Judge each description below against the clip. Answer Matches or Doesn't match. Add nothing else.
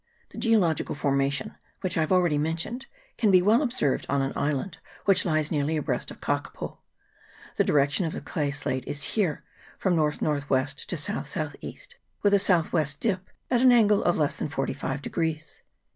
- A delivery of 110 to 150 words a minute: Doesn't match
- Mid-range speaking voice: Matches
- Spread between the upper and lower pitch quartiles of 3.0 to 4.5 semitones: Doesn't match